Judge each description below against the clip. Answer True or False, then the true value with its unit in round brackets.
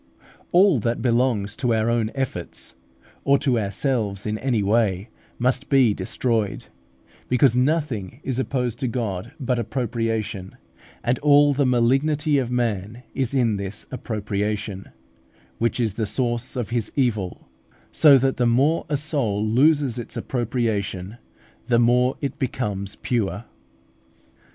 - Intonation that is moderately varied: True (3.7 semitones)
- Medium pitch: False (120 Hz)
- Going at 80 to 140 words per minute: True (135 wpm)